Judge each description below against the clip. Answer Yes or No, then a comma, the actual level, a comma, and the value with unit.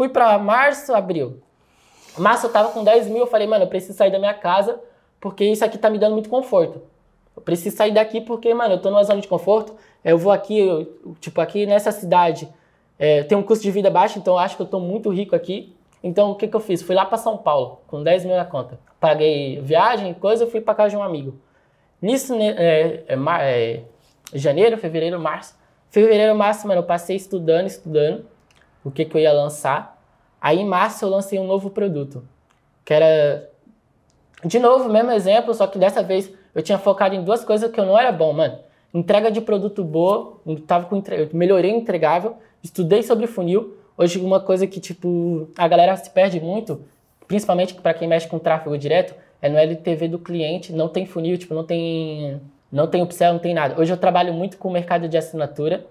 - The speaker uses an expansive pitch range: No, average, 4.4 semitones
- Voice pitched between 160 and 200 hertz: Yes, medium, 185 Hz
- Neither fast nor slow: No, fast, 210 wpm